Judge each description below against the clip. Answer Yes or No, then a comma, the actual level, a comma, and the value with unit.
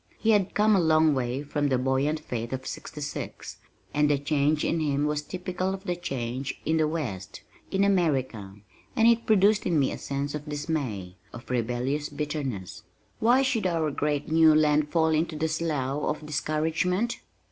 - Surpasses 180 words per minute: No, average, 175 wpm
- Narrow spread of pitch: No, average, 3.5 semitones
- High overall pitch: No, medium, 150 Hz